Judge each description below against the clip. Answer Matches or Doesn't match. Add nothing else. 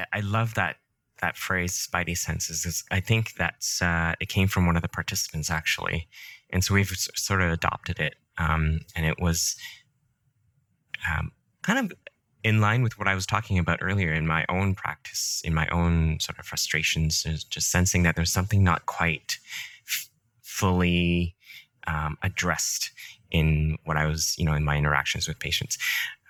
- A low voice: Matches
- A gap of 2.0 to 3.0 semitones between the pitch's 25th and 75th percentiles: Doesn't match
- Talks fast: Doesn't match